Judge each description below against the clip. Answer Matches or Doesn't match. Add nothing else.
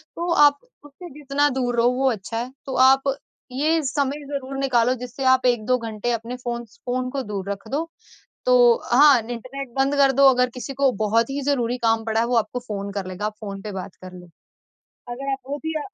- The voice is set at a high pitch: Matches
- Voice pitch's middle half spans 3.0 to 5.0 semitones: Matches